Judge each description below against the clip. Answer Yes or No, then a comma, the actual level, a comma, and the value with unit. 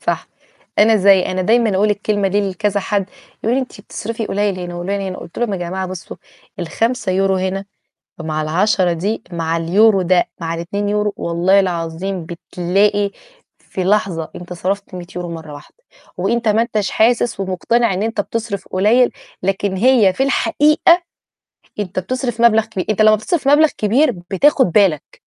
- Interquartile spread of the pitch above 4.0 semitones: No, average, 3.3 semitones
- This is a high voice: Yes, high, 200 Hz